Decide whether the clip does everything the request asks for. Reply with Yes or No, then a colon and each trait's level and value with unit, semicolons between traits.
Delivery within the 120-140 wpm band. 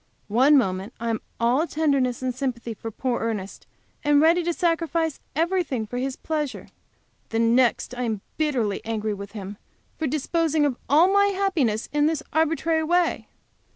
No: average, 160 wpm